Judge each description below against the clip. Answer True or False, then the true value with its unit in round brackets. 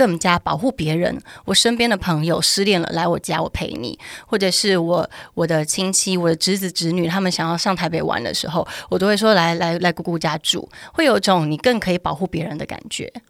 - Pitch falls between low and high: True (175 Hz)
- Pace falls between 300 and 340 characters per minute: True (325 characters per minute)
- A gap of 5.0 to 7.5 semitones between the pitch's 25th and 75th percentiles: False (2.7 semitones)